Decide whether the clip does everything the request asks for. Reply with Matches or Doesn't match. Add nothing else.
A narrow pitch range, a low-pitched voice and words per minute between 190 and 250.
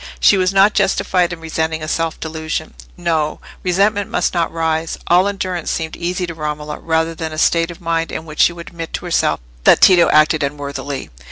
Doesn't match